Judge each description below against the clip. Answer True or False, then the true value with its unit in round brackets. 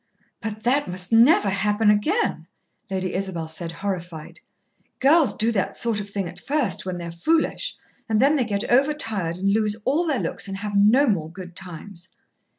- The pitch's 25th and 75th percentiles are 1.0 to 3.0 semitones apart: False (4.6 semitones)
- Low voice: False (205 Hz)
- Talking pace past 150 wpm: True (180 wpm)